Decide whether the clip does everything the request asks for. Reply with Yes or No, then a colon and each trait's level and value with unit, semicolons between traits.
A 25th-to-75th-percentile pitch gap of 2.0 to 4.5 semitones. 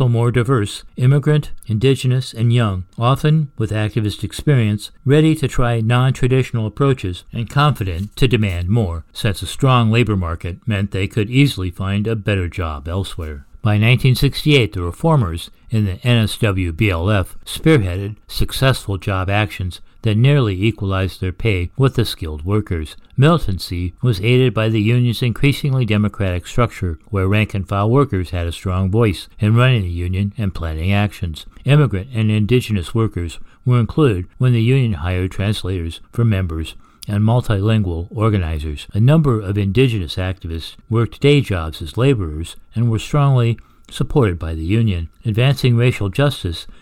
No: average, 4.9 semitones